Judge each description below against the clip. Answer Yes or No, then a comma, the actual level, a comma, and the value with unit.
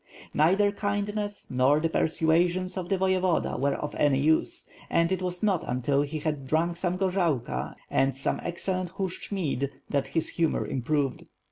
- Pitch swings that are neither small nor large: Yes, average, 4.3 semitones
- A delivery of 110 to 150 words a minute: No, average, 160 wpm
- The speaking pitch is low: No, medium, 170 Hz